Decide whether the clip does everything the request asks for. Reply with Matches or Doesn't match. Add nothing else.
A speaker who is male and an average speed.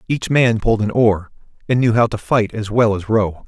Doesn't match